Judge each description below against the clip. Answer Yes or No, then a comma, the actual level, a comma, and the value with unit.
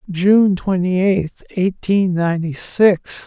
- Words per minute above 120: No, slow, 110 wpm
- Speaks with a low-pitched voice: No, medium, 185 Hz